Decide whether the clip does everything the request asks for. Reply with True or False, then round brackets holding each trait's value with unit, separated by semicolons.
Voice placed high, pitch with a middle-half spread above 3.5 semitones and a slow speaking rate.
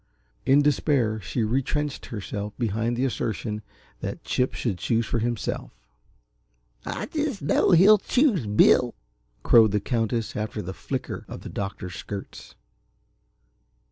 False (115 Hz; 4.7 semitones; 130 wpm)